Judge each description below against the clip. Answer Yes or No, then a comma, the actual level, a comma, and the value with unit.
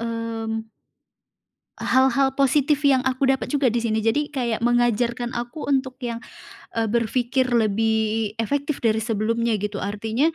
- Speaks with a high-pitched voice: Yes, high, 235 Hz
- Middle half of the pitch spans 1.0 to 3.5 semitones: Yes, average, 2.9 semitones